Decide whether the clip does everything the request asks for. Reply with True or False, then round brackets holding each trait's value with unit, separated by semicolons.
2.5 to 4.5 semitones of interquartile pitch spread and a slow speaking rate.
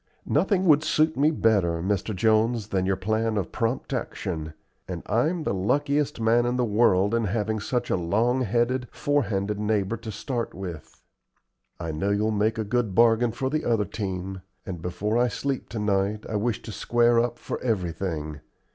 False (3.7 semitones; 180 wpm)